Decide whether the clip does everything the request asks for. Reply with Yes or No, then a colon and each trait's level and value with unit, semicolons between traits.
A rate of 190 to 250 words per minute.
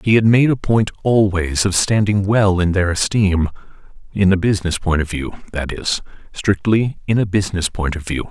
Yes: average, 195 wpm